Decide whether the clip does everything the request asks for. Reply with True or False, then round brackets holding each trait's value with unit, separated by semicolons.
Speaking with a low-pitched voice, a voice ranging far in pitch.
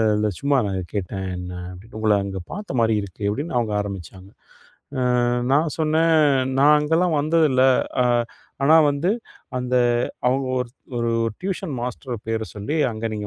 True (125 Hz; 6.6 semitones)